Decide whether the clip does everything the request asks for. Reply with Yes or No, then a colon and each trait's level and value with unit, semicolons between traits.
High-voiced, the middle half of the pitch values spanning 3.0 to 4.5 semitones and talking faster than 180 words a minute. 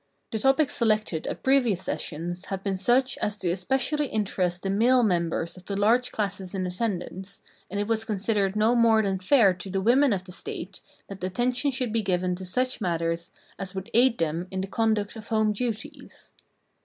Yes: high, 205 Hz; average, 3.9 semitones; average, 190 wpm